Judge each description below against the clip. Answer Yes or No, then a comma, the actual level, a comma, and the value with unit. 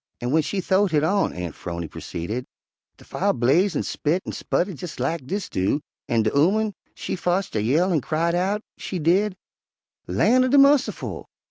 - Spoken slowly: No, average, 190 wpm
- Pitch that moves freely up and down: Yes, wide, 7.4 semitones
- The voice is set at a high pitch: No, medium, 170 Hz